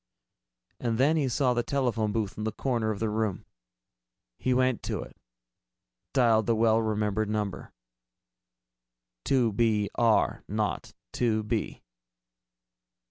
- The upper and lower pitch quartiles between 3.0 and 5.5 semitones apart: No, narrow, 2.4 semitones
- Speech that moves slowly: Yes, slow, 130 wpm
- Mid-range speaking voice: No, low, 110 Hz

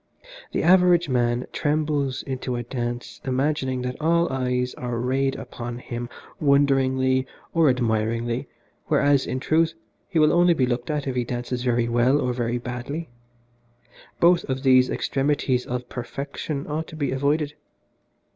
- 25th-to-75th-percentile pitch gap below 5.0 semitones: Yes, average, 3.1 semitones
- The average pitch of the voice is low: Yes, low, 130 Hz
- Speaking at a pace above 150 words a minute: No, average, 145 wpm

